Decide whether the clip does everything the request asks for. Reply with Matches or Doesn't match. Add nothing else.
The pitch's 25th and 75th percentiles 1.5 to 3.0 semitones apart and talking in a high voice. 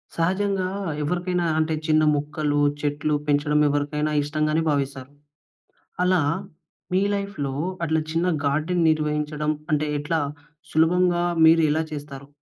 Doesn't match